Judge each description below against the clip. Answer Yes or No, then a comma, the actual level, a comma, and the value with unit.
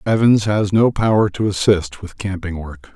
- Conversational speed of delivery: Yes, average, 185 wpm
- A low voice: Yes, low, 100 Hz